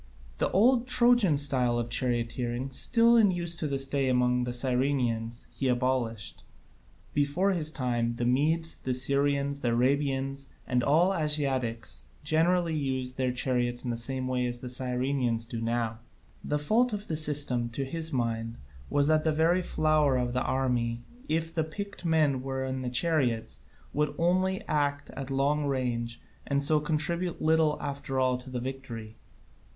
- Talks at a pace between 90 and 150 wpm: No, average, 165 wpm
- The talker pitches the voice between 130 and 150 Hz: Yes, low, 135 Hz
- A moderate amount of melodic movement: Yes, average, 4.0 semitones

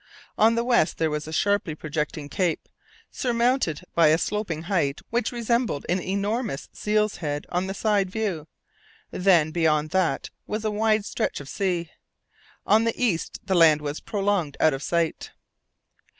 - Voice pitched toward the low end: No, medium, 185 Hz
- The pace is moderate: Yes, average, 160 wpm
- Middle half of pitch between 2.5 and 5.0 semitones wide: No, wide, 5.4 semitones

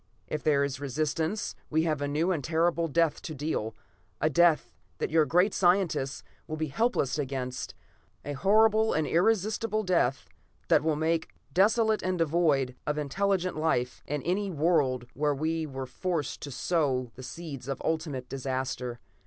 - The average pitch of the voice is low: No, medium, 155 Hz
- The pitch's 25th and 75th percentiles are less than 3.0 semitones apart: No, average, 4.3 semitones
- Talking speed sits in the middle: Yes, average, 160 wpm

